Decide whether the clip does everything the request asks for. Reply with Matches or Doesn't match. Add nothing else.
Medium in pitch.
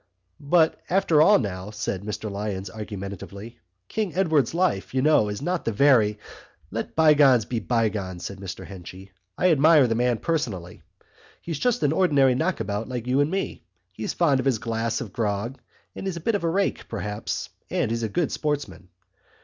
Doesn't match